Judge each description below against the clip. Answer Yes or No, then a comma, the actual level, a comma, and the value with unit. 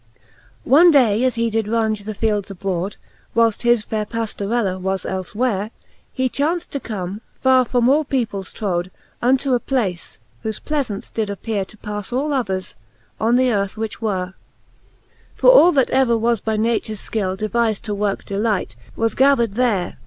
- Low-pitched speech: No, high, 220 Hz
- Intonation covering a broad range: No, average, 3.7 semitones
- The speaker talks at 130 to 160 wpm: No, average, 175 wpm